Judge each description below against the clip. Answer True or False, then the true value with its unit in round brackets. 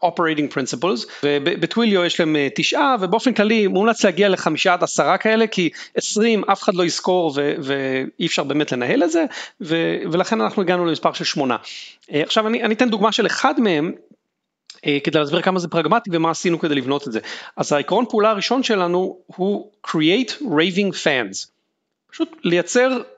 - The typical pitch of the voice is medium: True (180 Hz)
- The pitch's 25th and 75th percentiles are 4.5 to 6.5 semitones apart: True (5.1 semitones)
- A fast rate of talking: True (165 wpm)